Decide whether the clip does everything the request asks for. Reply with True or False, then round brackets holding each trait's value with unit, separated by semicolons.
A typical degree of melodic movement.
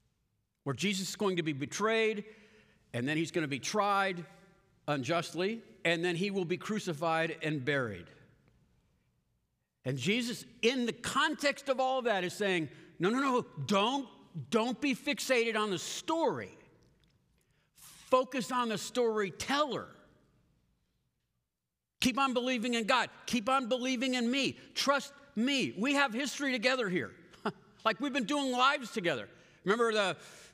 False (7.0 semitones)